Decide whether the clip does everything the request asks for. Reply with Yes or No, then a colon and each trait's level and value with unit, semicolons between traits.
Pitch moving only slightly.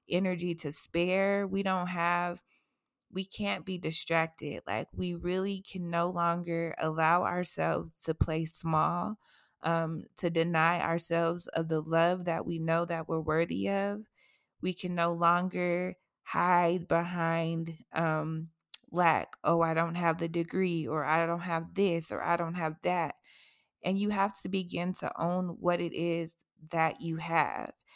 Yes: narrow, 1.6 semitones